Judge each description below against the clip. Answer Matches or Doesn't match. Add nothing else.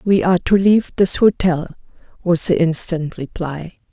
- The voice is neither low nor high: Matches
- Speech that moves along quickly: Doesn't match